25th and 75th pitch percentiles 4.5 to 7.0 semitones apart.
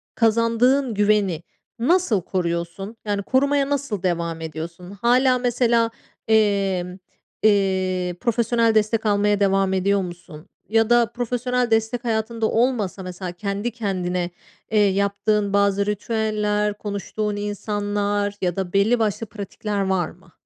No: average, 3.1 semitones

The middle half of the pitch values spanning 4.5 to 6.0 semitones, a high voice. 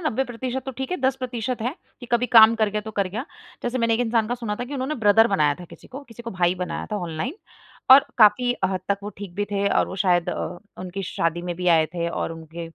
Yes: average, 5.1 semitones; high, 215 Hz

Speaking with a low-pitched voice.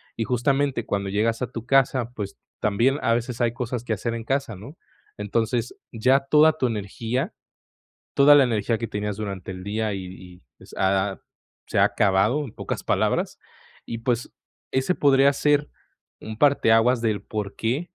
Yes: low, 115 Hz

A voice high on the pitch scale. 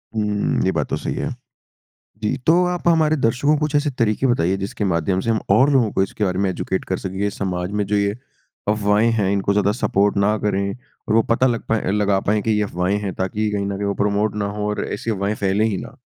No: low, 105 Hz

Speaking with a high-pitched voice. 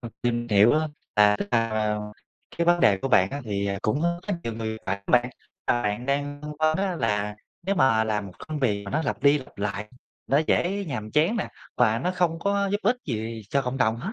No: low, 125 Hz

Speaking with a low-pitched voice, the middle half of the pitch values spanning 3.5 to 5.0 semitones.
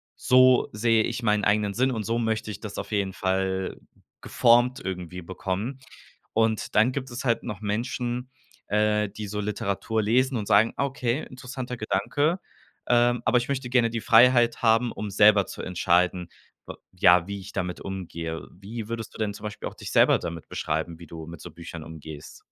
Yes: low, 105 Hz; average, 4.1 semitones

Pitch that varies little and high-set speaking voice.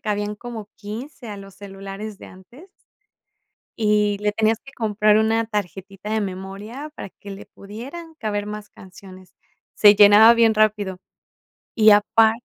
Yes: narrow, 1.9 semitones; high, 210 Hz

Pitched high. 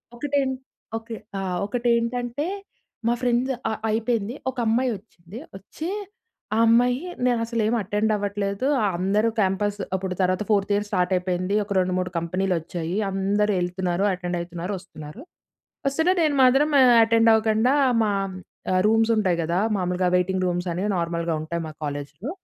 Yes: high, 200 Hz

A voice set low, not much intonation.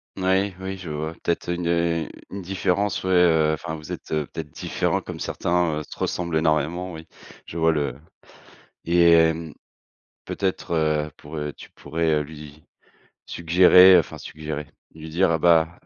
Yes: very low, 80 Hz; narrow, 2.2 semitones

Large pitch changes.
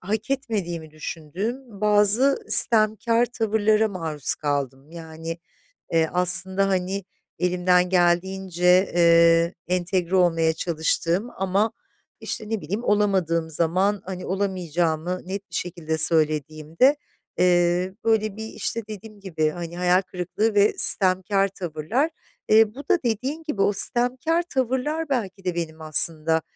No: average, 4.3 semitones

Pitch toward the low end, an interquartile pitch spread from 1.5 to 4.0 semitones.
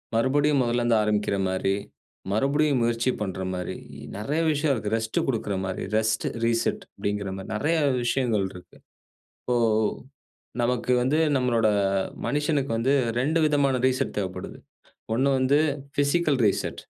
No: low, 120 Hz; average, 4.9 semitones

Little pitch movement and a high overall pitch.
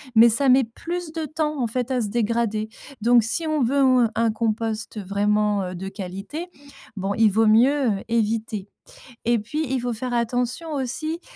No: average, 3.8 semitones; high, 235 Hz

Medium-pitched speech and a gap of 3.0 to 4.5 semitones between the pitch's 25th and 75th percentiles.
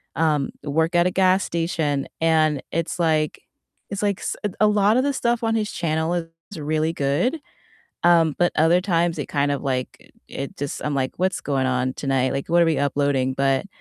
Yes: medium, 160 Hz; average, 3.9 semitones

